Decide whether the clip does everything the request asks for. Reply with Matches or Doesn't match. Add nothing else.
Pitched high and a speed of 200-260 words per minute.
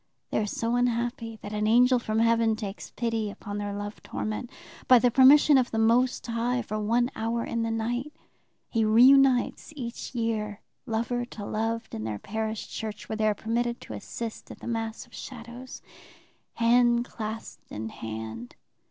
Doesn't match